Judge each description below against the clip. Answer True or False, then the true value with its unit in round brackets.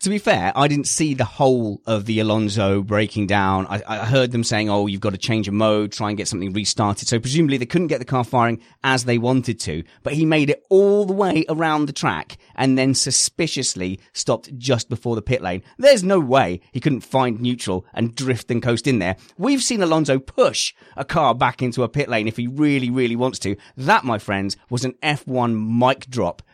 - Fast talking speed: True (225 wpm)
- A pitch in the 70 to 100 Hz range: False (125 Hz)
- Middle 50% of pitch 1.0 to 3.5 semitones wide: False (4.3 semitones)